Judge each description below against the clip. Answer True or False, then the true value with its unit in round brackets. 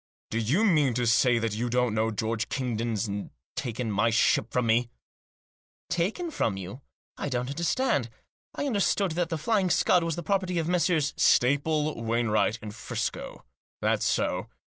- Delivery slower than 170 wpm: False (175 wpm)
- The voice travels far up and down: True (6.8 semitones)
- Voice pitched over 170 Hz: False (125 Hz)